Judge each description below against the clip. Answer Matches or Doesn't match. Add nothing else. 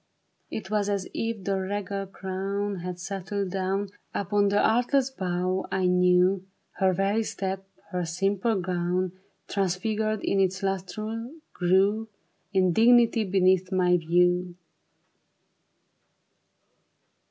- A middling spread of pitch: Doesn't match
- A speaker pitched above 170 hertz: Matches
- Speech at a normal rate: Doesn't match